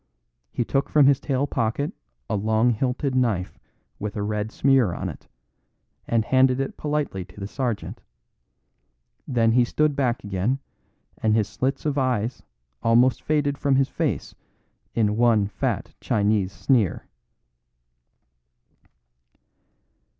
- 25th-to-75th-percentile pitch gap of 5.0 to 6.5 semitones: No, average, 4.0 semitones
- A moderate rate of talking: No, slow, 130 wpm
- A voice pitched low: Yes, low, 120 Hz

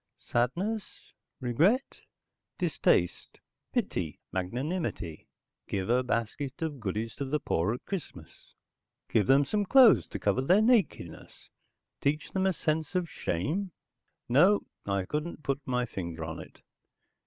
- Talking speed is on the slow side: Yes, slow, 130 wpm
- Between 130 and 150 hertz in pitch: Yes, medium, 140 Hz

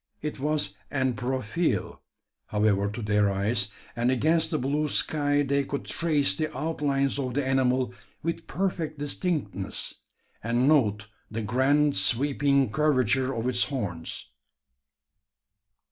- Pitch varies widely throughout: No, average, 4.5 semitones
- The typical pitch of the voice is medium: No, low, 130 Hz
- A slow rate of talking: Yes, slow, 125 wpm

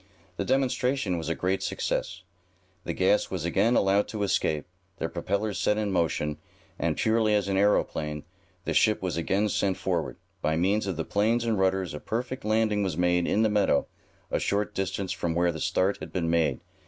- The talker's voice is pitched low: Yes, very low, 95 Hz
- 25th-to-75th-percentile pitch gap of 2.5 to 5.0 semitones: Yes, average, 3.4 semitones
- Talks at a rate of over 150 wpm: Yes, average, 190 wpm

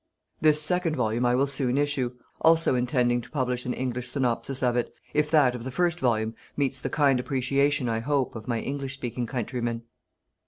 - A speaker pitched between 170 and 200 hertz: No, low, 130 Hz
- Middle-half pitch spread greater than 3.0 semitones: No, average, 2.7 semitones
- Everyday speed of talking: Yes, average, 190 wpm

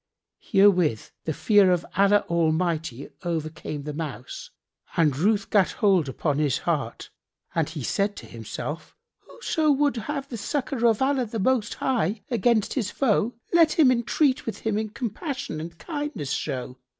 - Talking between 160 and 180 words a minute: No, average, 150 wpm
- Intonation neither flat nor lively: No, wide, 7.5 semitones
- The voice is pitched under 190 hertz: No, high, 200 Hz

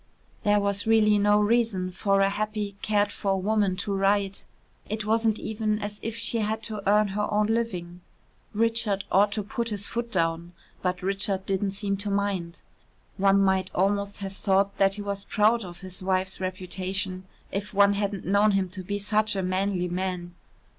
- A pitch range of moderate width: No, narrow, 1.8 semitones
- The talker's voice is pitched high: Yes, high, 200 Hz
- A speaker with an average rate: Yes, average, 180 wpm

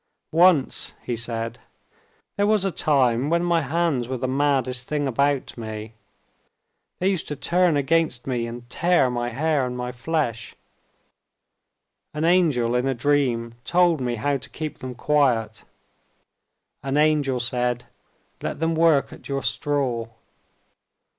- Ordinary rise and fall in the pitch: Yes, average, 4.4 semitones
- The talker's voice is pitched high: No, low, 135 Hz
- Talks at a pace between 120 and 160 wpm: Yes, average, 140 wpm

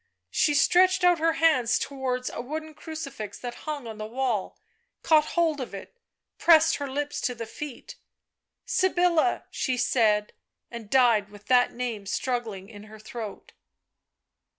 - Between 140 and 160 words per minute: Yes, average, 150 wpm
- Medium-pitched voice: No, very high, 255 Hz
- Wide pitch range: Yes, wide, 5.8 semitones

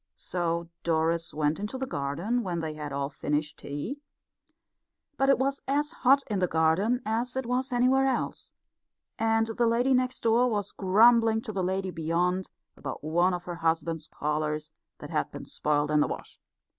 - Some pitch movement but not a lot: No, wide, 7.3 semitones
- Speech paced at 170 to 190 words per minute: Yes, average, 175 wpm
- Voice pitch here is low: No, medium, 185 Hz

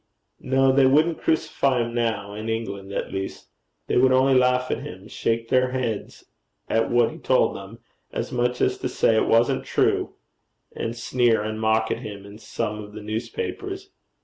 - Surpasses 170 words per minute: Yes, average, 180 wpm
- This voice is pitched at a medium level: No, low, 115 Hz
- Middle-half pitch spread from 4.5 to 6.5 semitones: No, average, 3.0 semitones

